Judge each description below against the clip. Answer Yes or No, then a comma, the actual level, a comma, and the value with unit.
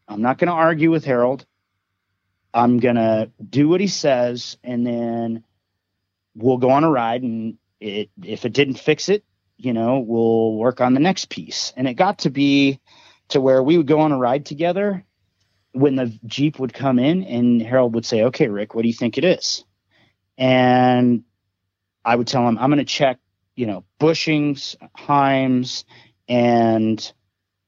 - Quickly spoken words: No, average, 180 wpm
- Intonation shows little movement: No, average, 3.9 semitones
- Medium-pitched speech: No, low, 120 Hz